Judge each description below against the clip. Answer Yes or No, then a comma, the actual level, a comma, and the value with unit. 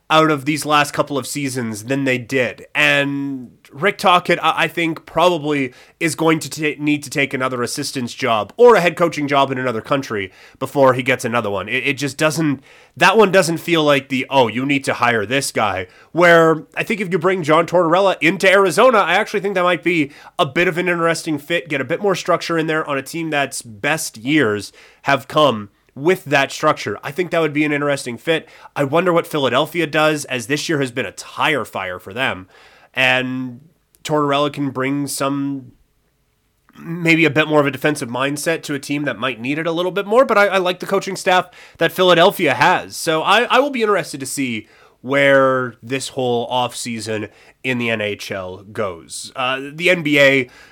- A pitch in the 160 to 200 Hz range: No, medium, 145 Hz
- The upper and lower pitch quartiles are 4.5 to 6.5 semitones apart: No, average, 4.1 semitones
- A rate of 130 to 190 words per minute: No, fast, 205 wpm